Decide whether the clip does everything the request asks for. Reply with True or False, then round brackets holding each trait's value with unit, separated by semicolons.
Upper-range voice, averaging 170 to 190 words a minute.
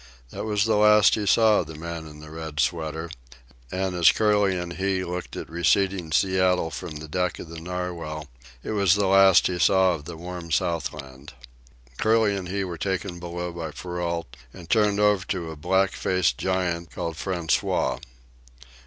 False (90 Hz; 180 wpm)